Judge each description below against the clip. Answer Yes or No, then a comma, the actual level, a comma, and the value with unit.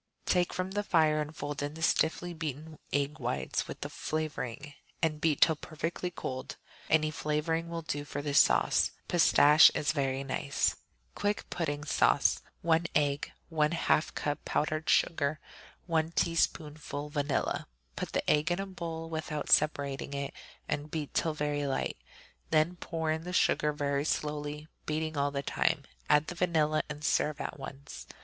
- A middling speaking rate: Yes, average, 160 wpm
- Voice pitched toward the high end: No, medium, 155 Hz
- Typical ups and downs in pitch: No, narrow, 1.9 semitones